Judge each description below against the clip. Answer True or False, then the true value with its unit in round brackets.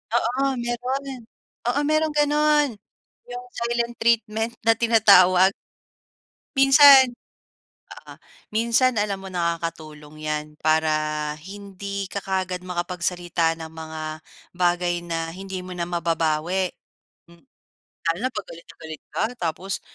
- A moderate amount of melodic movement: False (5.8 semitones)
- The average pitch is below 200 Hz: True (190 Hz)